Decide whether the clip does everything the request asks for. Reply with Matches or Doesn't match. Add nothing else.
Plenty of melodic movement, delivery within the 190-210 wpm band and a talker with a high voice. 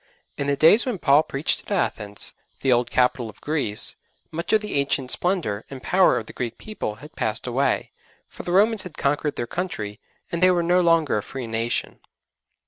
Doesn't match